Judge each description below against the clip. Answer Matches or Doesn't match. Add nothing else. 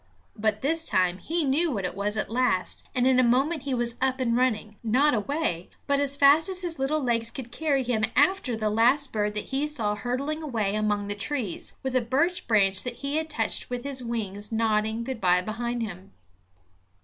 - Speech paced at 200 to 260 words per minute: Matches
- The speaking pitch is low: Doesn't match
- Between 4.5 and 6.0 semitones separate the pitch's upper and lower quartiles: Matches